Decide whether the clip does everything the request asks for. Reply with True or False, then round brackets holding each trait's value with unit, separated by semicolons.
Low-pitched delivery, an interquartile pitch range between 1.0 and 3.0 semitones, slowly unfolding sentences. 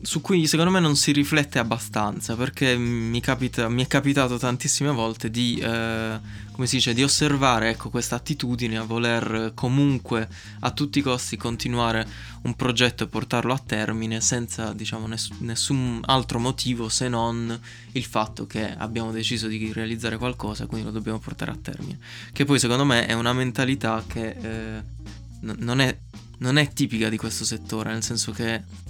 False (115 Hz; 2.7 semitones; 170 wpm)